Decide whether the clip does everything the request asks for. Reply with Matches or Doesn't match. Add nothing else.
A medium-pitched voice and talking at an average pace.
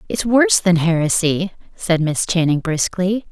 Matches